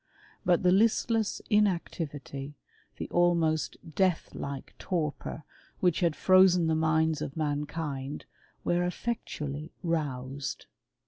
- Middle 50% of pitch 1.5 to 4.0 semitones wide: Yes, average, 3.5 semitones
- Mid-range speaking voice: Yes, medium, 160 Hz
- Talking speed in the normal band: No, slow, 100 wpm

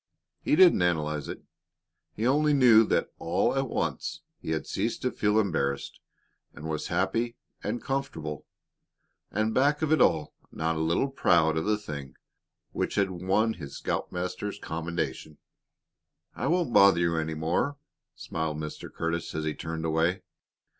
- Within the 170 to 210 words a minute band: No, average, 155 wpm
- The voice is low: Yes, very low, 90 Hz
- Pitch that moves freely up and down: Yes, wide, 5.9 semitones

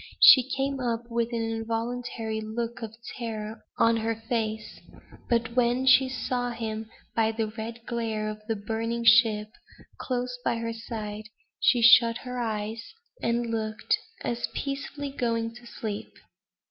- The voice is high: Yes, high, 230 Hz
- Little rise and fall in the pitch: Yes, narrow, 1.6 semitones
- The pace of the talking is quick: No, average, 145 wpm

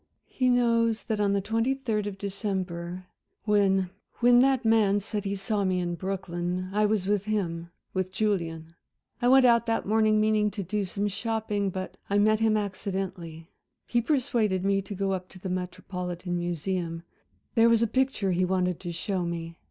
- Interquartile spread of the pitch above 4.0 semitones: No, average, 3.1 semitones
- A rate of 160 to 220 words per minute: Yes, average, 180 wpm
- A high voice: Yes, high, 200 Hz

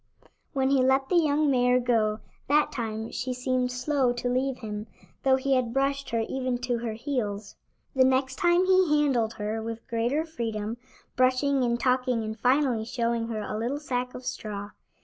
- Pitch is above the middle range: Yes, very high, 250 Hz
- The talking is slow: No, average, 180 wpm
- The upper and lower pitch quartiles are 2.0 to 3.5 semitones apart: Yes, average, 2.9 semitones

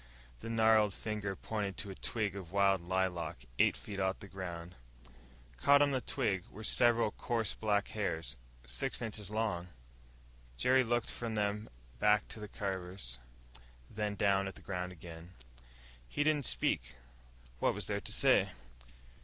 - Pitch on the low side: Yes, low, 100 Hz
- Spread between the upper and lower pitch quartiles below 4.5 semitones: Yes, average, 3.3 semitones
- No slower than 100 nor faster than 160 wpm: Yes, average, 155 wpm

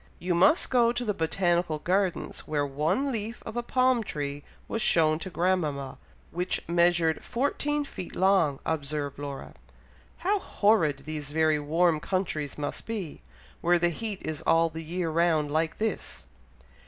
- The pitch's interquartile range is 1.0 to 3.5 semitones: No, average, 4.8 semitones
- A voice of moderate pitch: Yes, medium, 170 Hz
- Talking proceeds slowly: No, average, 155 wpm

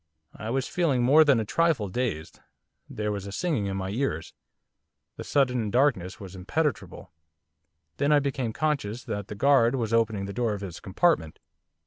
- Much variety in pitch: Yes, wide, 5.8 semitones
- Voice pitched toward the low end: Yes, low, 115 Hz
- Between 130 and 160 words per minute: No, average, 170 wpm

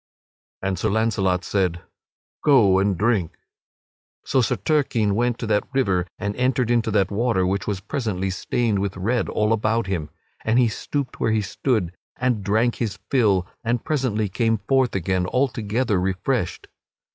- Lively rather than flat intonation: No, average, 3.9 semitones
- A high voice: No, low, 110 Hz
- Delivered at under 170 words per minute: Yes, average, 155 wpm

